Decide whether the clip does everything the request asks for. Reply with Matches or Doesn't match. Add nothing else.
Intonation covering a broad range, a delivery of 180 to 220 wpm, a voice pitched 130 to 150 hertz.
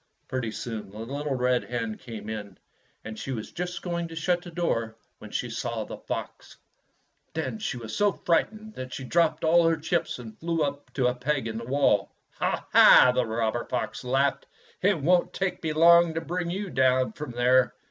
Matches